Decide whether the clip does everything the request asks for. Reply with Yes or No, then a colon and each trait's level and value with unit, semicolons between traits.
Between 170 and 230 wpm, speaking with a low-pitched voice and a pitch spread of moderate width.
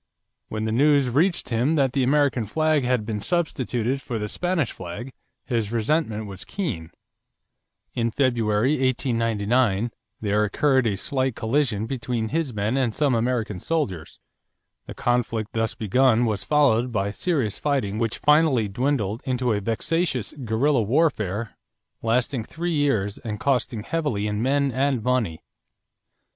No: average, 140 wpm; low, 120 Hz; average, 4.4 semitones